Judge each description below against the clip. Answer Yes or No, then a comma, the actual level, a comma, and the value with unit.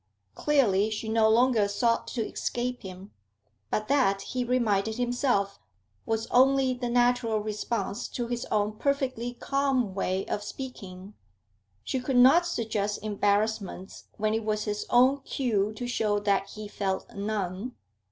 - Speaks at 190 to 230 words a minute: No, average, 140 wpm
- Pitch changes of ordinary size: Yes, average, 3.4 semitones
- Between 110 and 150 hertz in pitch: No, high, 220 Hz